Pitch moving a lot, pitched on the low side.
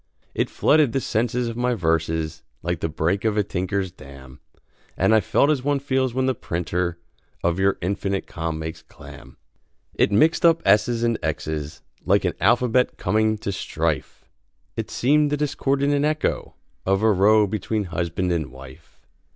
Yes: wide, 6.7 semitones; low, 100 Hz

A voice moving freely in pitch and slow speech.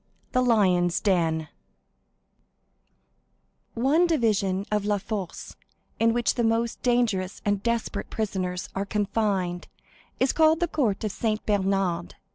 No: average, 3.7 semitones; slow, 120 wpm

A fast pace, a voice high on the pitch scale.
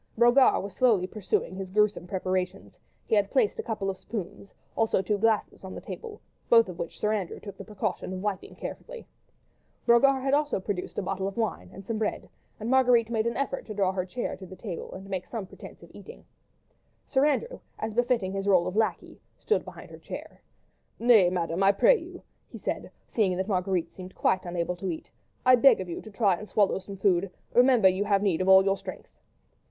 Yes: fast, 210 wpm; high, 200 Hz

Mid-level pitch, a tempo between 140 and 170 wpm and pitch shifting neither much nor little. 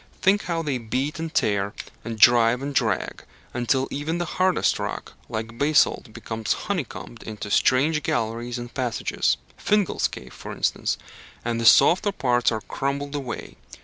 No: low, 130 Hz; average, 150 wpm; average, 4.9 semitones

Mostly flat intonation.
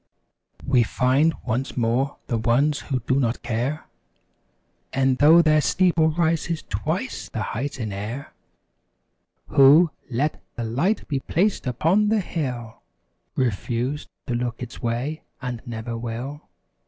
No: average, 4.4 semitones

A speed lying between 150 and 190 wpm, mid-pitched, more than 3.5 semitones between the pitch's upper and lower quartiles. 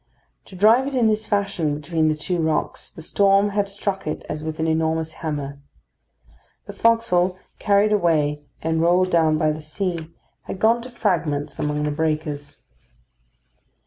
Yes: average, 160 wpm; medium, 165 Hz; average, 4.5 semitones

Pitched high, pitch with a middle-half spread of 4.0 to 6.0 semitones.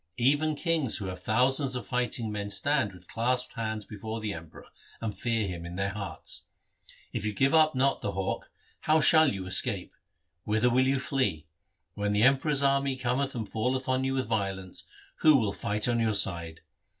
No: low, 115 Hz; average, 4.7 semitones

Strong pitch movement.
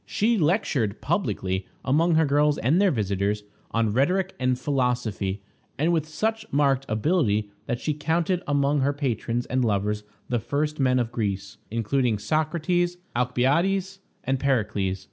Yes: wide, 6.2 semitones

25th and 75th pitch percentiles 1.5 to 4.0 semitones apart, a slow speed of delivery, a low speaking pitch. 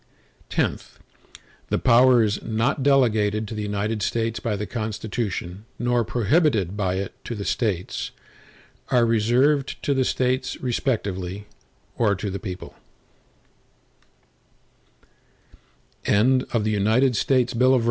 Yes: average, 3.2 semitones; slow, 95 wpm; low, 110 Hz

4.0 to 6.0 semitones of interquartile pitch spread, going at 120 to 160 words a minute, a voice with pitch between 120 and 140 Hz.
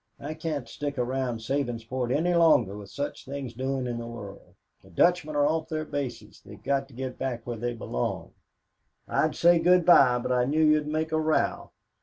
No: average, 4.4 semitones; average, 195 wpm; low, 135 Hz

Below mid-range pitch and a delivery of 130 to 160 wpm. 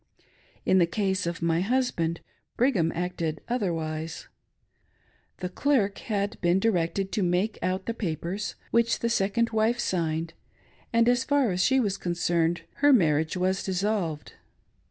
No: high, 190 Hz; average, 150 wpm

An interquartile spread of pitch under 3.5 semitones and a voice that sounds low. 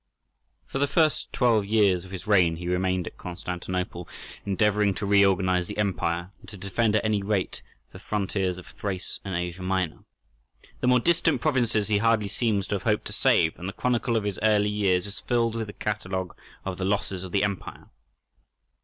Yes: average, 2.7 semitones; low, 100 Hz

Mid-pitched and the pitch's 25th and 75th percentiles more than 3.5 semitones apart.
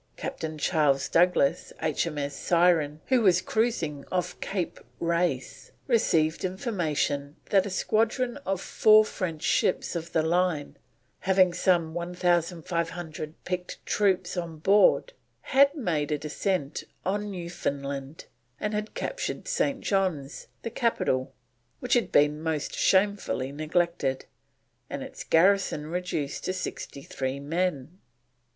Yes: medium, 175 Hz; average, 4.2 semitones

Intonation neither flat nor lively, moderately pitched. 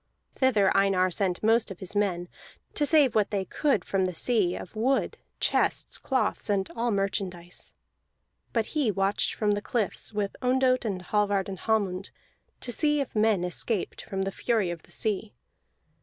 No: average, 3.4 semitones; high, 205 Hz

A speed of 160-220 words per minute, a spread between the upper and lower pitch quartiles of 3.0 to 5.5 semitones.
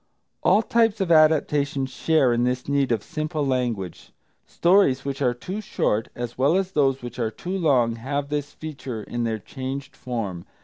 Yes: average, 175 wpm; average, 4.1 semitones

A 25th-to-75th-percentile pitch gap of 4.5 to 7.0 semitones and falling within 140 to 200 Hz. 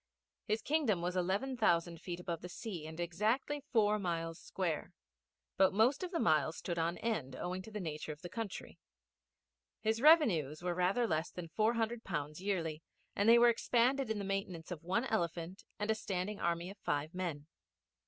Yes: average, 4.8 semitones; medium, 185 Hz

